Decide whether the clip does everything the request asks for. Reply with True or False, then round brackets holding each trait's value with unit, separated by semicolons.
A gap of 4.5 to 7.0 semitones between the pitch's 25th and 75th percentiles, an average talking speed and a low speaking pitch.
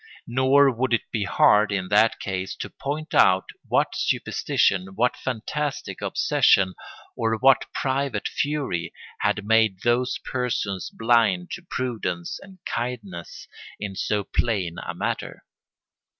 False (5.2 semitones; 125 wpm; 115 Hz)